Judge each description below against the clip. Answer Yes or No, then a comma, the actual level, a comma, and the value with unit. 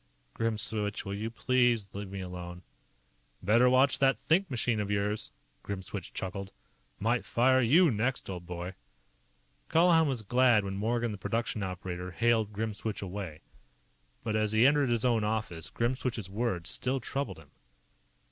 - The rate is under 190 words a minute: Yes, average, 145 wpm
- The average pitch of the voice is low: Yes, low, 110 Hz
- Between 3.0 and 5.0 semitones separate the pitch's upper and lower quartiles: Yes, average, 3.9 semitones